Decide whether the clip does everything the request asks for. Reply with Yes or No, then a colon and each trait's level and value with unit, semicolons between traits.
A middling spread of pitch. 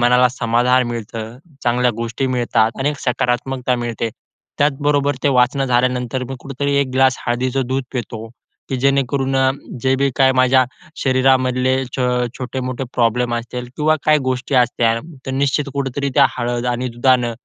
No: narrow, 1.7 semitones